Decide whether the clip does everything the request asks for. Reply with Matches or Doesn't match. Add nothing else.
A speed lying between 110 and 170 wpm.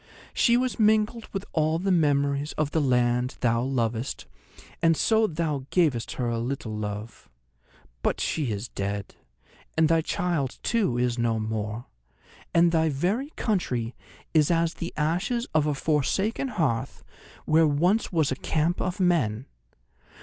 Matches